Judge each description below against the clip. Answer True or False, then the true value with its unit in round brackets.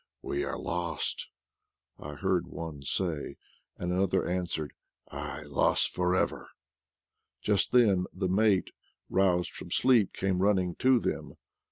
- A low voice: True (90 Hz)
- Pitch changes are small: True (2.0 semitones)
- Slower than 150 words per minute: True (135 wpm)